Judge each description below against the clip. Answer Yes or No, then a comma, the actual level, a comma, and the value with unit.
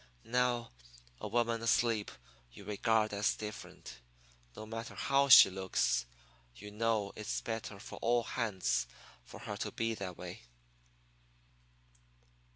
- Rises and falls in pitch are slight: Yes, narrow, 2.3 semitones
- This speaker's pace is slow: Yes, slow, 125 wpm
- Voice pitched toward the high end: No, low, 110 Hz